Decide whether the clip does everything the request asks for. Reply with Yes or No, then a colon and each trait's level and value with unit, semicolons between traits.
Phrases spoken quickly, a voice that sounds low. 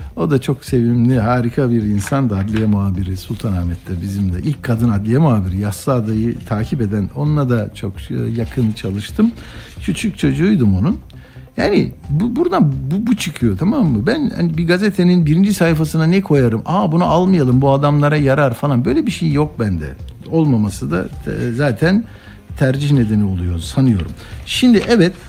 Yes: fast, 155 wpm; low, 130 Hz